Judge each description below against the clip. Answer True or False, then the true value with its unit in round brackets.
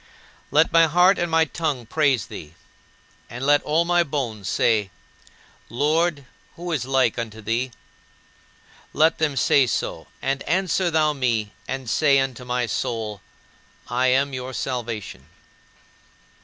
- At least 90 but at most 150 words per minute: True (140 wpm)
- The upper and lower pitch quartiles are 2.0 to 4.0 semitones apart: False (4.8 semitones)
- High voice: False (135 Hz)